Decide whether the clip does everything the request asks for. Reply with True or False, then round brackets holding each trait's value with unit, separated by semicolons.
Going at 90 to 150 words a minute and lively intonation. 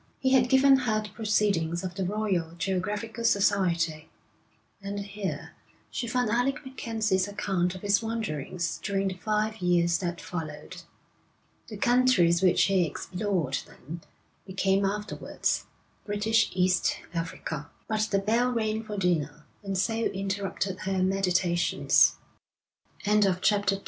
False (135 wpm; 3.2 semitones)